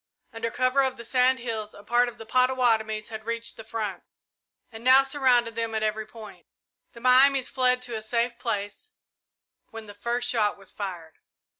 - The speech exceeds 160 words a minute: Yes, average, 180 wpm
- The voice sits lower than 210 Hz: No, high, 230 Hz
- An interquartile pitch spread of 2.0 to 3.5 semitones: Yes, narrow, 2.6 semitones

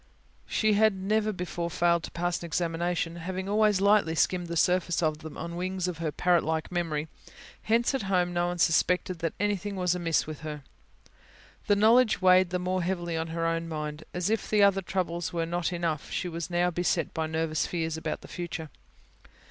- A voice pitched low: No, medium, 175 Hz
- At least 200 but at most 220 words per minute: Yes, fast, 205 wpm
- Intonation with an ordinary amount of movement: No, narrow, 2.2 semitones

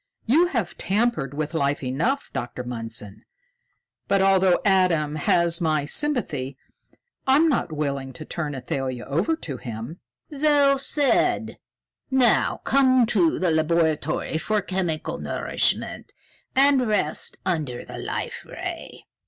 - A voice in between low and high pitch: Yes, medium, 170 Hz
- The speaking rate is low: Yes, slow, 120 wpm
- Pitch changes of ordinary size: No, wide, 9.0 semitones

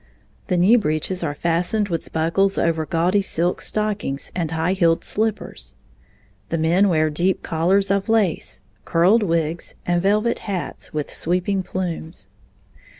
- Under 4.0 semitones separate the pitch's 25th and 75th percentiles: Yes, average, 3.2 semitones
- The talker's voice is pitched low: No, medium, 175 Hz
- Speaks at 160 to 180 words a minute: No, average, 140 wpm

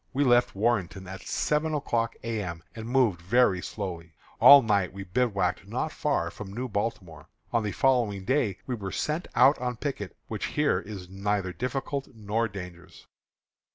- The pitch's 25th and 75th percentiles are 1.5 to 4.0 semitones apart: No, average, 4.6 semitones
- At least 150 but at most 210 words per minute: Yes, average, 165 wpm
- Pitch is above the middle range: No, low, 105 Hz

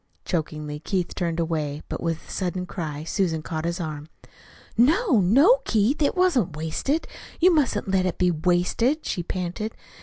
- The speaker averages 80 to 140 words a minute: No, average, 160 wpm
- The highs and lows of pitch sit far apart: Yes, wide, 6.5 semitones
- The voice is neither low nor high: Yes, medium, 180 Hz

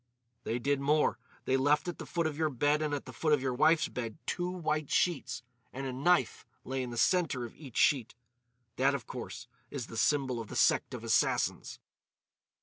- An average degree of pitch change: Yes, average, 3.4 semitones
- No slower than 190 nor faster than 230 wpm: Yes, fast, 205 wpm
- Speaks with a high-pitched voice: No, medium, 140 Hz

